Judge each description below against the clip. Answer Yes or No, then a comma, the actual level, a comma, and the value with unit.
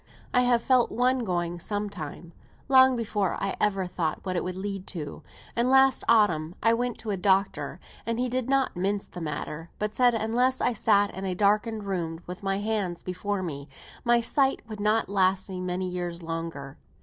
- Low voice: No, high, 200 Hz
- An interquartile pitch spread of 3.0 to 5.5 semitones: Yes, average, 4.4 semitones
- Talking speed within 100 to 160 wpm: No, average, 195 wpm